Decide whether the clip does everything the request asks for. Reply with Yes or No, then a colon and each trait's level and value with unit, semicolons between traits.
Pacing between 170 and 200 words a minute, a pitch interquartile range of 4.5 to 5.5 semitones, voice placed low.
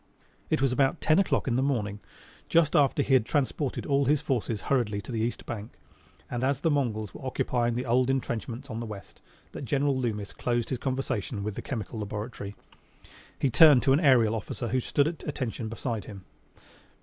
No: average, 195 wpm; average, 3.6 semitones; low, 125 Hz